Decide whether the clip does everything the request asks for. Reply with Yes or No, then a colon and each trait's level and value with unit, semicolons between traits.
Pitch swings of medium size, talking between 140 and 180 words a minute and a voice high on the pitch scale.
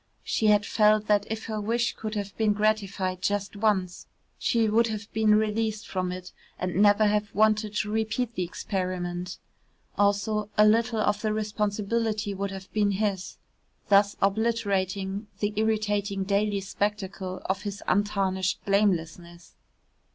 No: narrow, 1.8 semitones; average, 145 wpm; high, 205 Hz